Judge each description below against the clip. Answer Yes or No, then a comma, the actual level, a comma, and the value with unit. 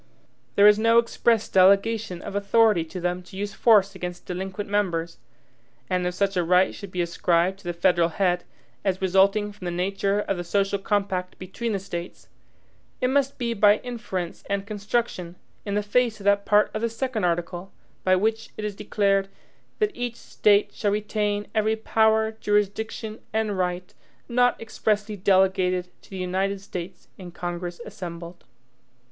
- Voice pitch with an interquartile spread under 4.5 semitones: Yes, average, 2.8 semitones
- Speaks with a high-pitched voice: Yes, high, 200 Hz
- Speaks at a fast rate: No, average, 165 wpm